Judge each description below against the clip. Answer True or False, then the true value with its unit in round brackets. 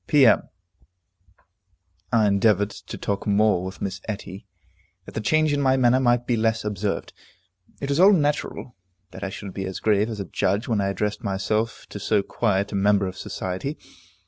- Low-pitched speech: True (105 Hz)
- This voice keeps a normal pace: True (180 wpm)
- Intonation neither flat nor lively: True (3.5 semitones)